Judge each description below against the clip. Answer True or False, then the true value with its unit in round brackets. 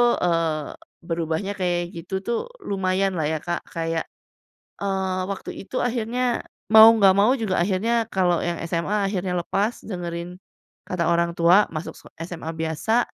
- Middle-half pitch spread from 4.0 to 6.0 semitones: False (3.0 semitones)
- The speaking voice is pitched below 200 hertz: True (185 Hz)